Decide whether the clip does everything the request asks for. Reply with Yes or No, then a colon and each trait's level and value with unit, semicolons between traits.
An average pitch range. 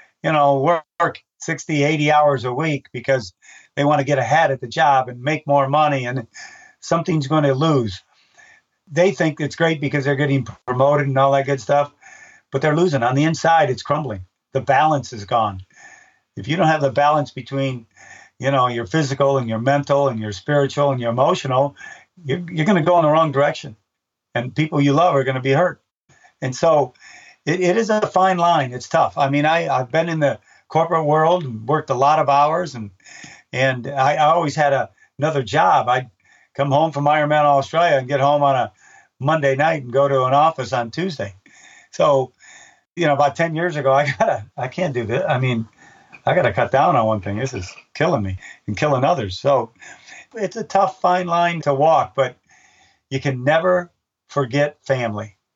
Yes: average, 3.5 semitones